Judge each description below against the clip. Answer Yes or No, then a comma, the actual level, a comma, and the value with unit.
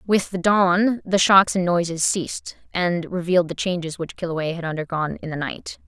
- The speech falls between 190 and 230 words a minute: Yes, average, 195 wpm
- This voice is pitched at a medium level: Yes, medium, 175 Hz